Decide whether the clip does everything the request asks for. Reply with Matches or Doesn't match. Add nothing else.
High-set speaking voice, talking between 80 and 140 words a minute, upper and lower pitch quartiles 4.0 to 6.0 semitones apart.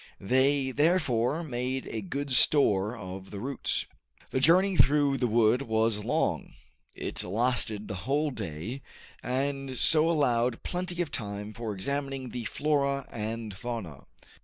Doesn't match